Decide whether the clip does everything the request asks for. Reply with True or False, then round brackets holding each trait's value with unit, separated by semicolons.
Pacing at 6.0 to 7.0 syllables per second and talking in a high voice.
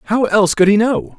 True (6.1 syllables/s; 205 Hz)